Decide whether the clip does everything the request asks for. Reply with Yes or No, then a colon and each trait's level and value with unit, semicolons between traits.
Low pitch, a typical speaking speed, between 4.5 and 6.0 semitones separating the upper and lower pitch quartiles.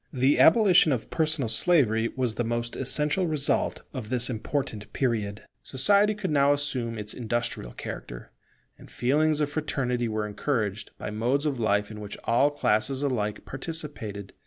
Yes: low, 125 Hz; average, 155 wpm; average, 5.1 semitones